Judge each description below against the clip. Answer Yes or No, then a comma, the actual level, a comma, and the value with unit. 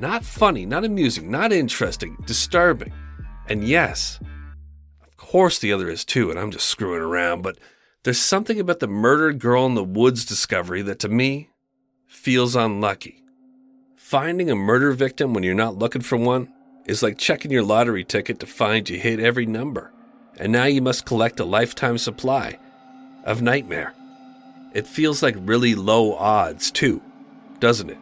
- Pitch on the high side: No, low, 125 Hz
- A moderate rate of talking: Yes, average, 165 wpm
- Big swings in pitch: Yes, wide, 7.2 semitones